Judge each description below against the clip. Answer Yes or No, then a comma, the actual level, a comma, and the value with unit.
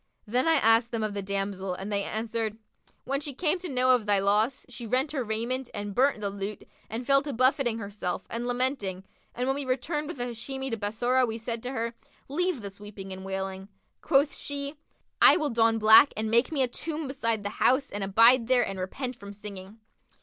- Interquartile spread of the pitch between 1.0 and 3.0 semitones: No, average, 4.4 semitones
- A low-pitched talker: No, high, 230 Hz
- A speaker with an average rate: No, fast, 215 wpm